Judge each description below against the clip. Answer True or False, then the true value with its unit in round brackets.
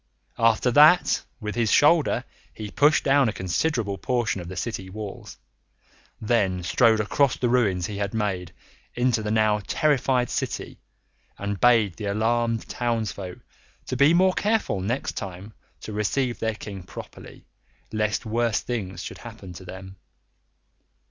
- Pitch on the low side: True (110 Hz)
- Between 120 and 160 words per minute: True (145 wpm)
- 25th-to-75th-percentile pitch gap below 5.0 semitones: True (3.6 semitones)